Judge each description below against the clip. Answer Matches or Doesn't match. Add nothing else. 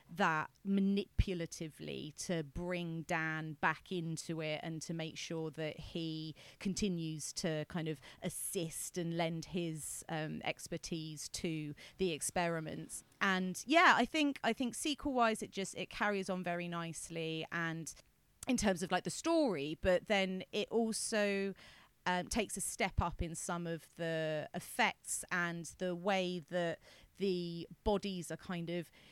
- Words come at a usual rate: Matches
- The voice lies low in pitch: Doesn't match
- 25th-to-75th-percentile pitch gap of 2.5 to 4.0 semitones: Matches